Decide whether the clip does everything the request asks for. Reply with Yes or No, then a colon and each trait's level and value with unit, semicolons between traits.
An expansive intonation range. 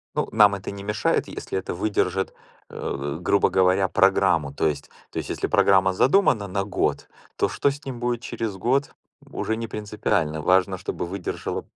No: average, 2.9 semitones